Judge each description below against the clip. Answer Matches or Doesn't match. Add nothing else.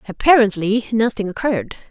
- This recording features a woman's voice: Matches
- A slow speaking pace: Matches